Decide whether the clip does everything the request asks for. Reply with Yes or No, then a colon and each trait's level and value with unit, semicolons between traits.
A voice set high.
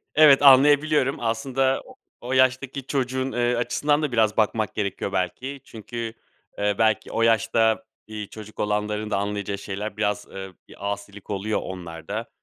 No: low, 110 Hz